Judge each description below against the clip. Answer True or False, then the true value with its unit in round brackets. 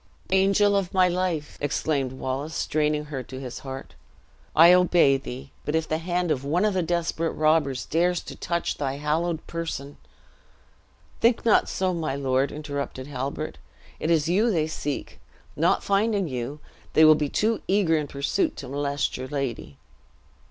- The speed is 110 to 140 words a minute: False (165 wpm)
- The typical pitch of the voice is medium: True (155 Hz)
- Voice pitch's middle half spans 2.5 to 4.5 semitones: True (4.1 semitones)